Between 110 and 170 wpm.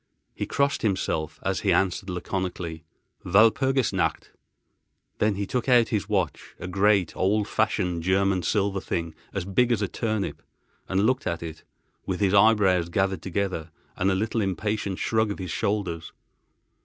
Yes: average, 155 wpm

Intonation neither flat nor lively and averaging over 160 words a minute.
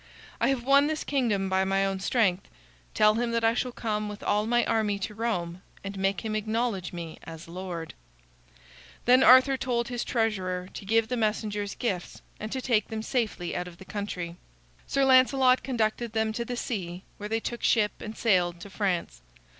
Yes: average, 3.8 semitones; average, 190 wpm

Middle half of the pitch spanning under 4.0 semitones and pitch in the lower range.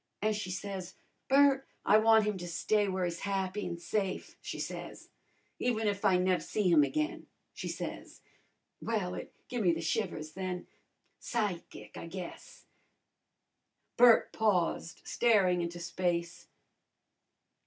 No: average, 3.6 semitones; high, 190 Hz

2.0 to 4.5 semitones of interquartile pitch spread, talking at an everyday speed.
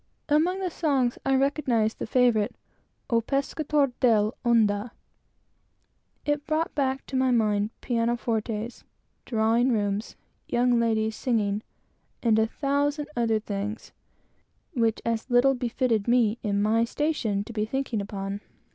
No: average, 3.6 semitones; slow, 130 wpm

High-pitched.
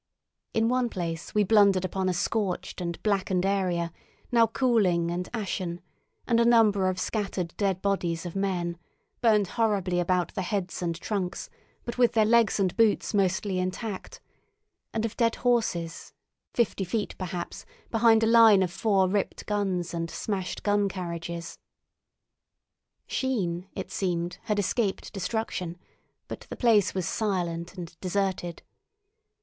Yes: high, 195 Hz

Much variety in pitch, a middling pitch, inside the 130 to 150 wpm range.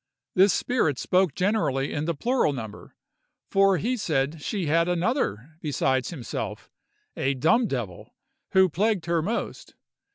Yes: wide, 6.2 semitones; medium, 165 Hz; slow, 135 wpm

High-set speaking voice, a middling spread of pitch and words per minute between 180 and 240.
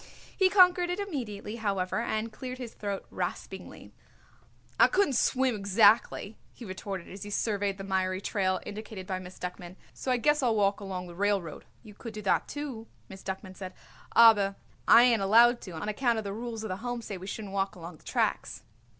Yes: high, 205 Hz; average, 3.6 semitones; average, 195 wpm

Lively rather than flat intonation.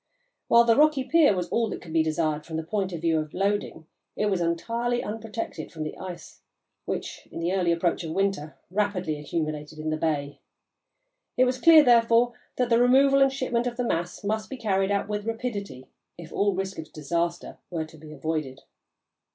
Yes: wide, 6.4 semitones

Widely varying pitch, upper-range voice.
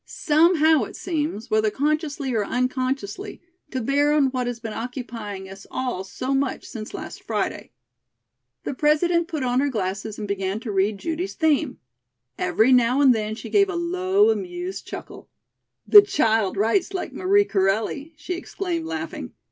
Yes: wide, 7.0 semitones; very high, 270 Hz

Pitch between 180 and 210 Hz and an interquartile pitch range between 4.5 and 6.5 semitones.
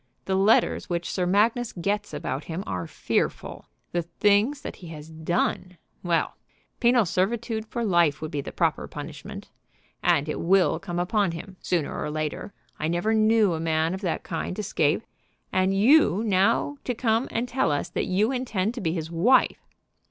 Yes: medium, 185 Hz; average, 4.9 semitones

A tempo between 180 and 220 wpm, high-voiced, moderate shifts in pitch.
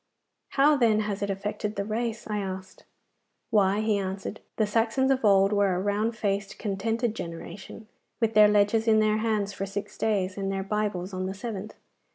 No: average, 185 wpm; high, 210 Hz; narrow, 2.0 semitones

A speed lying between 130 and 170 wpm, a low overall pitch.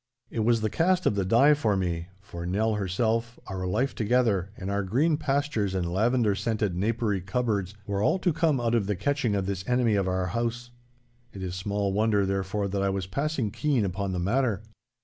No: fast, 205 wpm; low, 105 Hz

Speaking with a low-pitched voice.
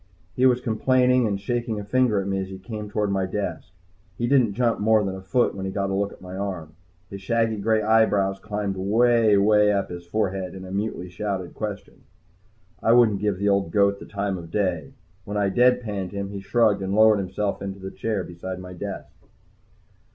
Yes: low, 100 Hz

